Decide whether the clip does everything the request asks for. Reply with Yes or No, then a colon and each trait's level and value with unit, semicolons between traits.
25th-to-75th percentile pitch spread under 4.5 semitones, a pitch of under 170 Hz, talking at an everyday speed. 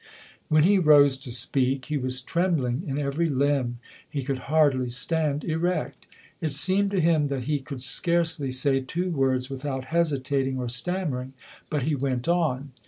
Yes: average, 3.7 semitones; medium, 140 Hz; average, 165 wpm